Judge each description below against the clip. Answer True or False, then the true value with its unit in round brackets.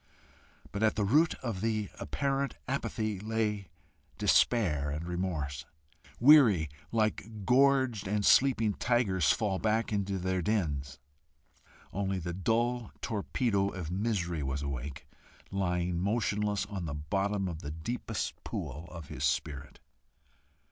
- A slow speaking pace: True (125 wpm)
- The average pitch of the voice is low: True (100 Hz)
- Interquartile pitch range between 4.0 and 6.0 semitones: True (4.8 semitones)